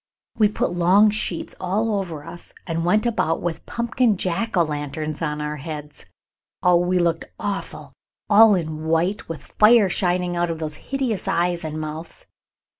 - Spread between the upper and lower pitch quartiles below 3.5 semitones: No, average, 4.3 semitones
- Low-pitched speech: No, medium, 175 Hz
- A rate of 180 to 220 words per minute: No, average, 165 wpm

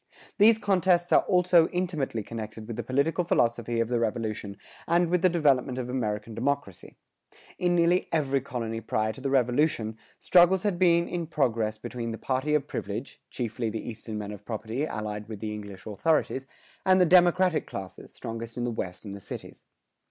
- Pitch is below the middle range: Yes, low, 125 Hz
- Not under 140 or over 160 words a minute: No, average, 180 wpm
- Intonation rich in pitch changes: Yes, wide, 7.4 semitones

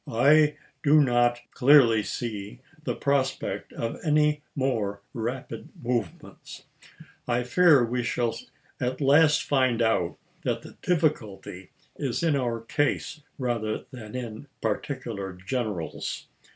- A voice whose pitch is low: Yes, low, 125 Hz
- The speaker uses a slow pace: Yes, slow, 115 wpm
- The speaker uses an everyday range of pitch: Yes, average, 4.1 semitones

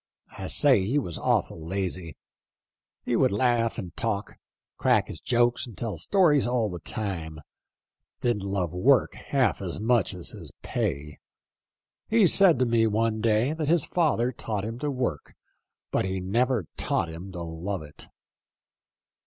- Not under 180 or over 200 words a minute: No, average, 160 wpm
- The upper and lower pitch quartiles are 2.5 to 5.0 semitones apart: No, wide, 5.4 semitones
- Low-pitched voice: Yes, low, 110 Hz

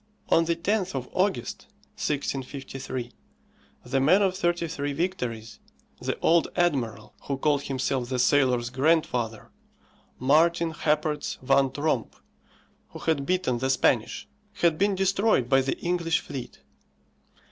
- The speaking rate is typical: No, slow, 125 wpm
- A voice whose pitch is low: No, medium, 145 Hz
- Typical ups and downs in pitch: Yes, average, 4.6 semitones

